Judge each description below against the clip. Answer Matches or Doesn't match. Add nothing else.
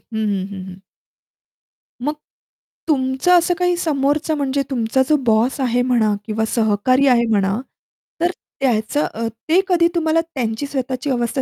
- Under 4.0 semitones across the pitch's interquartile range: Doesn't match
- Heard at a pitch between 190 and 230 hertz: Doesn't match